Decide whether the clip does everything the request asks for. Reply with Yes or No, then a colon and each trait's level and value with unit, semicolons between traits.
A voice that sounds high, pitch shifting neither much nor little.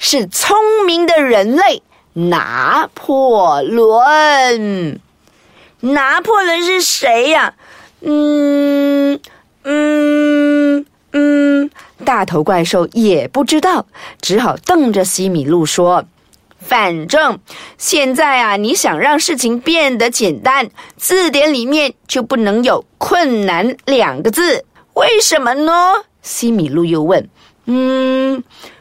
Yes: very high, 275 Hz; average, 4.7 semitones